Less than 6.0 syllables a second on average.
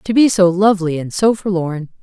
Yes: 5.5 syllables/s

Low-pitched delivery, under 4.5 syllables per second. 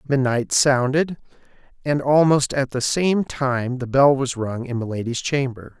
Yes: low, 130 Hz; 4.3 syllables/s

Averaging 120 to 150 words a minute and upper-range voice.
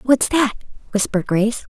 Yes: average, 140 wpm; high, 230 Hz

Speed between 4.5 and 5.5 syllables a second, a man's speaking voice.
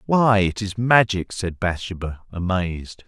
No: 4.2 syllables/s; male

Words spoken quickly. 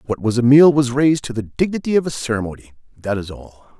Yes: fast, 235 wpm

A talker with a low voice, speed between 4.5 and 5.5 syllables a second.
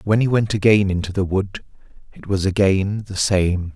Yes: low, 100 Hz; 5.1 syllables/s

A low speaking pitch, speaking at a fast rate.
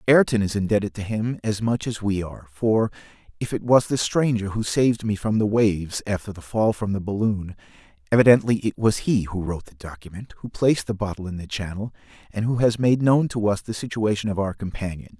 Yes: low, 105 Hz; fast, 215 wpm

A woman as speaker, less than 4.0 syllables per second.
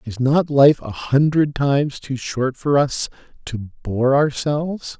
No: male; 3.8 syllables/s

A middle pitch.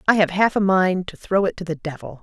Yes: medium, 180 Hz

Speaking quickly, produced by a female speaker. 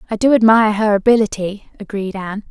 No: average, 170 wpm; female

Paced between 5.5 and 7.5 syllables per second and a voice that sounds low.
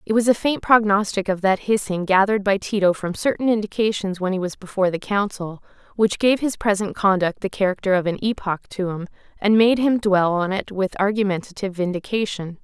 No: 5.7 syllables/s; high, 200 Hz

